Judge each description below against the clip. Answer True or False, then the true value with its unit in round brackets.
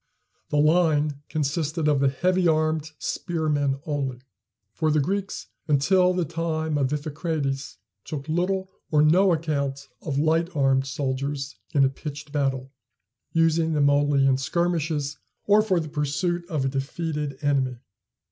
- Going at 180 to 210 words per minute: False (140 wpm)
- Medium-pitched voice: True (150 Hz)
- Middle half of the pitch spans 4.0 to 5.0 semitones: False (2.8 semitones)